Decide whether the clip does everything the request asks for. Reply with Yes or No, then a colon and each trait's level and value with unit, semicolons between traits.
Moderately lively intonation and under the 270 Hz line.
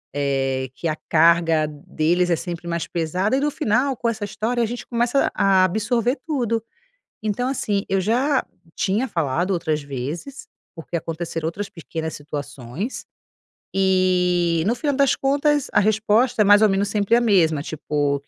No: wide, 6.3 semitones; high, 190 Hz